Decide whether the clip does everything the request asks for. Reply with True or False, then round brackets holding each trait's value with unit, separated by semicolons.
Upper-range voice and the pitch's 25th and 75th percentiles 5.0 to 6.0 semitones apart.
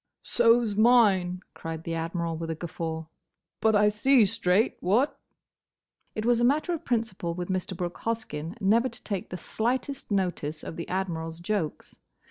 True (195 Hz; 5.3 semitones)